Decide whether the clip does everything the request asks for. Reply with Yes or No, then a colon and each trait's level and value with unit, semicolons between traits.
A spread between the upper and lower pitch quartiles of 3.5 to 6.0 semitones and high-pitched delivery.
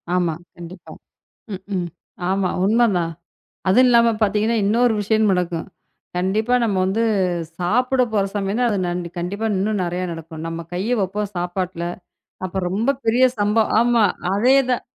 Yes: average, 4.1 semitones; high, 200 Hz